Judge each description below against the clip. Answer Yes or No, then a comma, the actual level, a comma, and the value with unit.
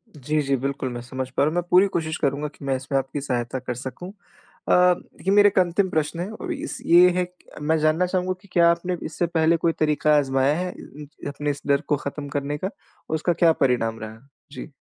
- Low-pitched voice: No, medium, 150 Hz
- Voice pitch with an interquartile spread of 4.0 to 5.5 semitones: Yes, average, 4.3 semitones